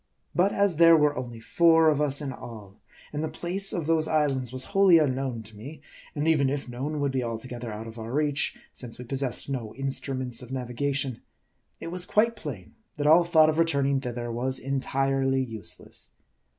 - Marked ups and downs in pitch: No, average, 4.1 semitones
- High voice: No, low, 135 Hz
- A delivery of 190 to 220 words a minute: Yes, average, 195 wpm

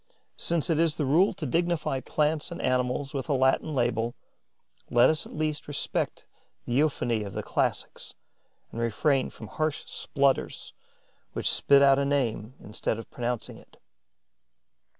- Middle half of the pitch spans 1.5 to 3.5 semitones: No, average, 4.2 semitones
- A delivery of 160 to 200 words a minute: No, average, 150 wpm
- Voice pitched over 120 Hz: Yes, medium, 140 Hz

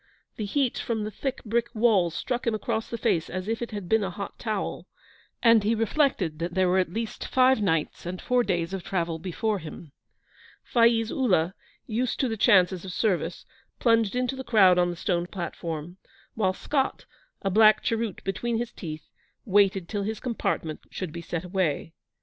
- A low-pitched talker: No, high, 205 Hz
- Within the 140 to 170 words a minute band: No, average, 185 wpm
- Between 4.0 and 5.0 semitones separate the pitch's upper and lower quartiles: Yes, average, 4.6 semitones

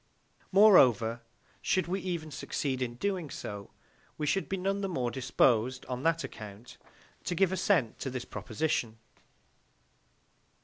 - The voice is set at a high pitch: No, medium, 140 Hz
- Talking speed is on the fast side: No, slow, 135 wpm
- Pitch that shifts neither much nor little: No, wide, 7.6 semitones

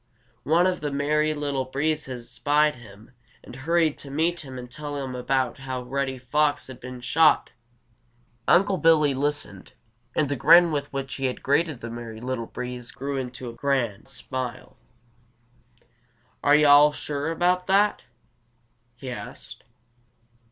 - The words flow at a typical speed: Yes, average, 150 wpm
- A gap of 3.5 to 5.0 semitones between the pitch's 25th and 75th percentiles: No, average, 3.1 semitones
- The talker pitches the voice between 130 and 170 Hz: Yes, medium, 140 Hz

